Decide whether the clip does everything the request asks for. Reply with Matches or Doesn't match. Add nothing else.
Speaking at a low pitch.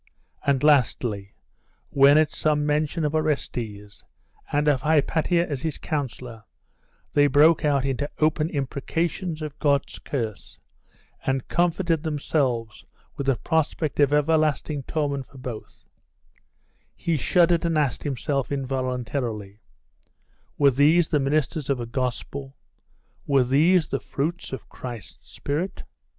Doesn't match